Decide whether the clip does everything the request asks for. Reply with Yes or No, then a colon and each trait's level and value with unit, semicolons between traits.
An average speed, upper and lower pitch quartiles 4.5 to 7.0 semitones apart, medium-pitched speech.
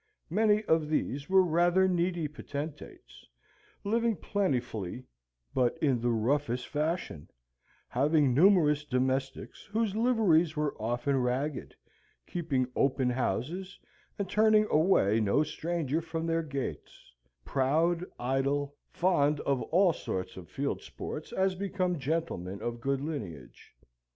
No: slow, 120 wpm; average, 5.1 semitones; medium, 150 Hz